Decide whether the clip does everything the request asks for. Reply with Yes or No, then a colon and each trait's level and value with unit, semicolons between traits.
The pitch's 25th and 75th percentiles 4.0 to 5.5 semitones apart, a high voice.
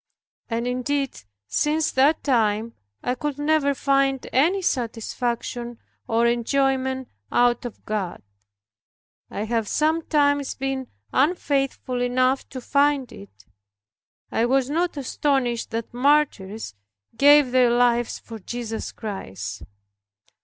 No: average, 3.3 semitones; very high, 255 Hz